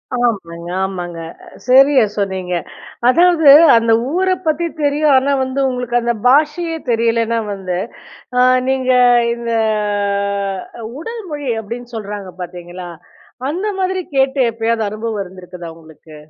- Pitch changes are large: Yes, wide, 6.7 semitones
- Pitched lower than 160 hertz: No, high, 235 Hz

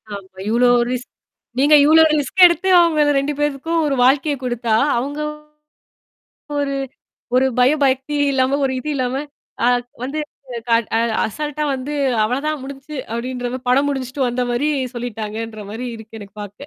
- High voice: Yes, very high, 265 Hz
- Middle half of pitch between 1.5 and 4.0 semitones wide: Yes, average, 3.3 semitones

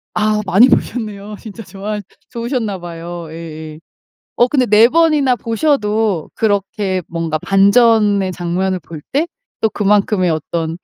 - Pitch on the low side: No, high, 205 Hz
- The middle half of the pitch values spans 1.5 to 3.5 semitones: No, average, 4.4 semitones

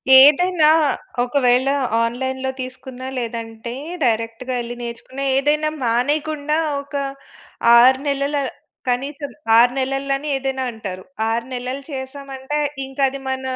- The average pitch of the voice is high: Yes, very high, 265 Hz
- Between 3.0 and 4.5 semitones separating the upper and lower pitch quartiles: No, narrow, 2.4 semitones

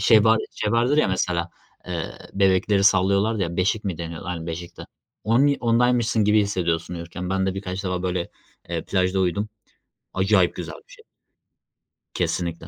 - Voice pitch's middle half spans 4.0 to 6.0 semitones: No, average, 3.3 semitones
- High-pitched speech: No, very low, 95 Hz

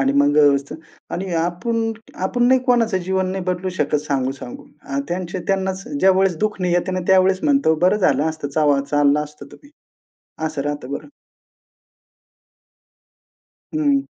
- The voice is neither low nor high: Yes, medium, 180 Hz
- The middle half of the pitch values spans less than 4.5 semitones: No, average, 4.8 semitones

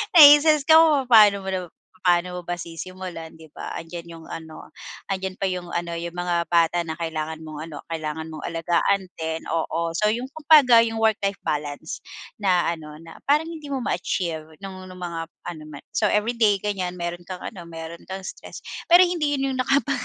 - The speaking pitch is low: No, medium, 180 Hz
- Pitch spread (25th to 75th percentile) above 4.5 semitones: Yes, wide, 5.4 semitones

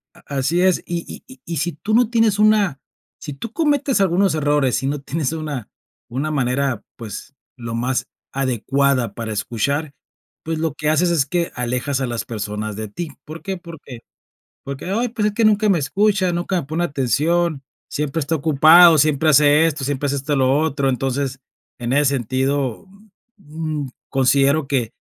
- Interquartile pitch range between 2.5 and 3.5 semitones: No, average, 4.4 semitones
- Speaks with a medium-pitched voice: Yes, medium, 145 Hz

